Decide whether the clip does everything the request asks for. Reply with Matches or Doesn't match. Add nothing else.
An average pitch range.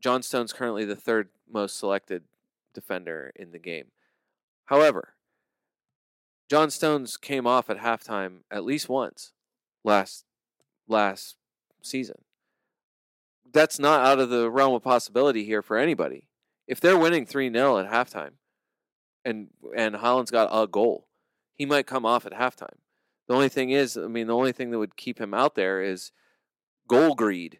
Matches